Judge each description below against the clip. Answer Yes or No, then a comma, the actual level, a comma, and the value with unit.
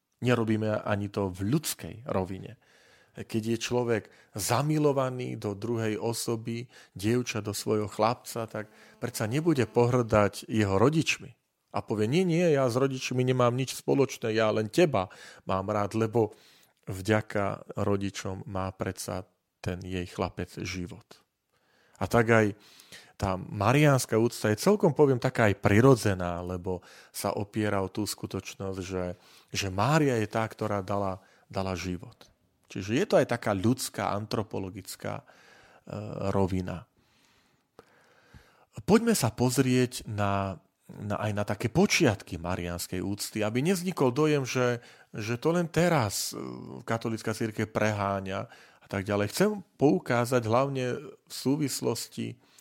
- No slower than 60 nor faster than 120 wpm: No, average, 130 wpm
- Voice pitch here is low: Yes, low, 110 Hz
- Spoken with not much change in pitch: No, average, 4.0 semitones